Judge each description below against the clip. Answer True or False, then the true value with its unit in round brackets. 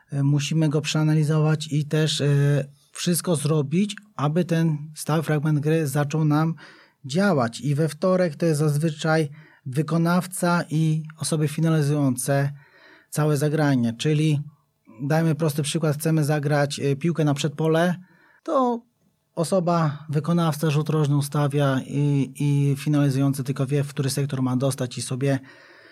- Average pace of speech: True (125 wpm)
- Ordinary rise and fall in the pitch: False (2.1 semitones)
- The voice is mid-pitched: True (155 Hz)